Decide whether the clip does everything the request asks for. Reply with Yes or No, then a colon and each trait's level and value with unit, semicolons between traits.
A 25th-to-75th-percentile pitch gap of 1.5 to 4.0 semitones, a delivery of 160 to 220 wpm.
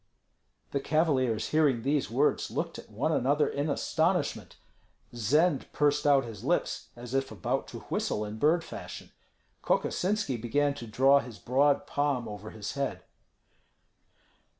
No: average, 3.7 semitones; average, 140 wpm